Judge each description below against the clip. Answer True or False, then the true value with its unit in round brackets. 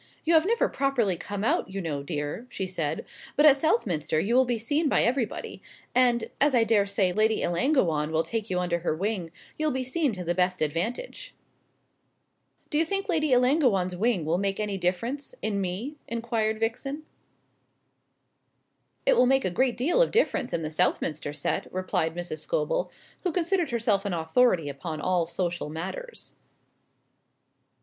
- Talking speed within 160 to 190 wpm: True (165 wpm)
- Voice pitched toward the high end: True (215 Hz)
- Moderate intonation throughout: False (7.3 semitones)